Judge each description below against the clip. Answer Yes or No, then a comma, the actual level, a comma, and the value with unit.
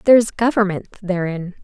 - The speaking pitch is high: Yes, high, 200 Hz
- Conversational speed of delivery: Yes, average, 145 wpm